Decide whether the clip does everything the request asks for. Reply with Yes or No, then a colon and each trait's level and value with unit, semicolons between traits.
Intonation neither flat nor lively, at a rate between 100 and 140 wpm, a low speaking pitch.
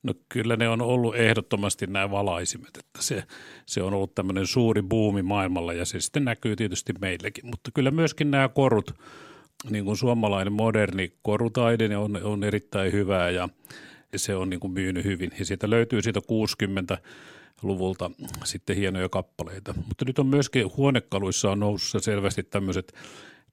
No: average, 3.3 semitones; fast, 155 wpm; low, 100 Hz